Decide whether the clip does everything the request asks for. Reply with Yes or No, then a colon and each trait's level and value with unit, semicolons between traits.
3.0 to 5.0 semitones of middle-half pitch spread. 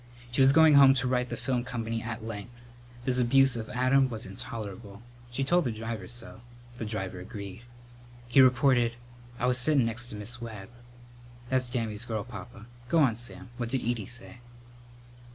No: narrow, 2.4 semitones